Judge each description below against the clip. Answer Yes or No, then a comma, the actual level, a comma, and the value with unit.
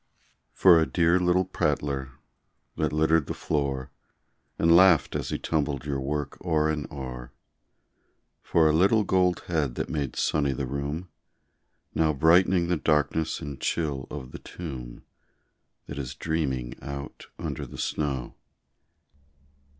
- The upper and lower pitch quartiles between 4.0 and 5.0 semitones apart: No, average, 3.2 semitones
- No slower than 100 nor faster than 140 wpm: Yes, slow, 135 wpm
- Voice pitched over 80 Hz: No, very low, 75 Hz